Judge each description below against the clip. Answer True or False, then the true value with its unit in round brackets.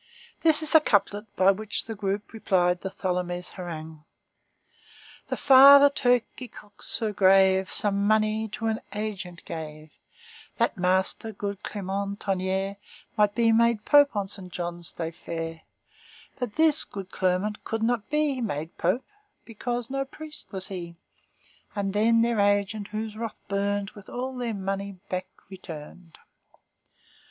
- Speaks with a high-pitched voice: True (205 Hz)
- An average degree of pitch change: True (3.4 semitones)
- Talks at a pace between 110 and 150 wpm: True (145 wpm)